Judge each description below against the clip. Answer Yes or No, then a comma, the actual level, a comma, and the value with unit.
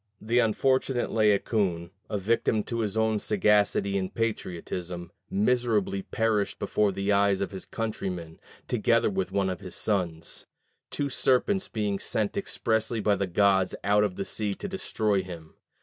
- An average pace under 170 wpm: Yes, average, 150 wpm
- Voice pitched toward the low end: Yes, low, 105 Hz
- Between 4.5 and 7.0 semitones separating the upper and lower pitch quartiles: No, average, 2.7 semitones